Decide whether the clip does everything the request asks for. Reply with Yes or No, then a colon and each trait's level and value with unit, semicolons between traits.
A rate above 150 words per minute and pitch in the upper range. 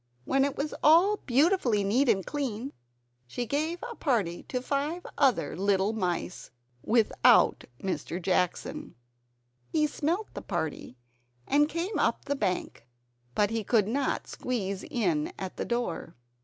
No: average, 140 wpm; high, 240 Hz